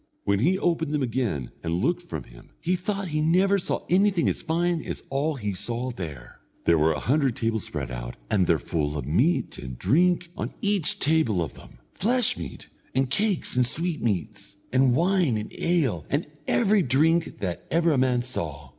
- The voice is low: Yes, low, 130 Hz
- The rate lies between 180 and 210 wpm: Yes, average, 190 wpm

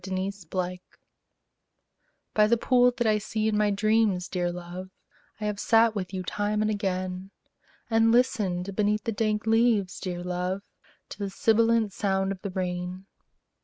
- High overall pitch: Yes, high, 200 Hz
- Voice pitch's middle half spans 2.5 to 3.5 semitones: Yes, average, 2.8 semitones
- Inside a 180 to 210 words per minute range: No, average, 160 wpm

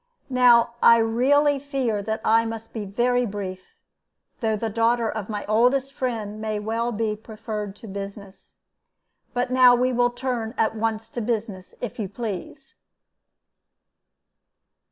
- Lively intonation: No, narrow, 2.4 semitones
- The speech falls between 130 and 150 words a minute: Yes, average, 140 wpm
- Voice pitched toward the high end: Yes, high, 225 Hz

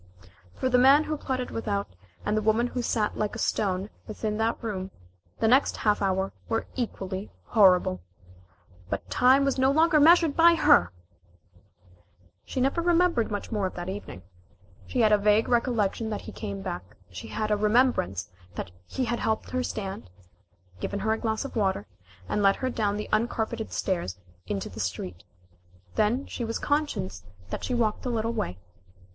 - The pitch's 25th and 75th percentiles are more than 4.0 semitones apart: Yes, average, 4.4 semitones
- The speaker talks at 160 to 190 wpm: Yes, average, 175 wpm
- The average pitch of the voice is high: Yes, high, 220 Hz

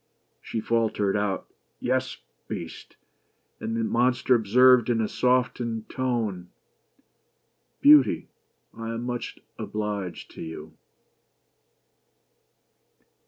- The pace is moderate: No, slow, 105 wpm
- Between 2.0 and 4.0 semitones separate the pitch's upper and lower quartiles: Yes, average, 3.3 semitones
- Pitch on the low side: Yes, low, 115 Hz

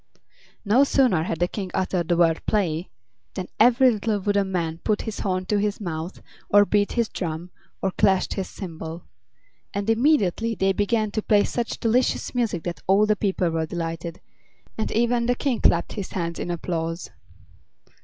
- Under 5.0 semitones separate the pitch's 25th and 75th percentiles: Yes, average, 4.2 semitones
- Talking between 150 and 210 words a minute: Yes, average, 175 wpm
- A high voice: Yes, high, 195 Hz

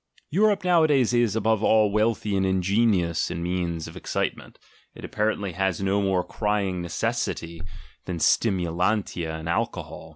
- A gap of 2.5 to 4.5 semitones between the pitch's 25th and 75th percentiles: Yes, average, 3.9 semitones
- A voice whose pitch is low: Yes, low, 100 Hz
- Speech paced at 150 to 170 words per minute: No, slow, 135 wpm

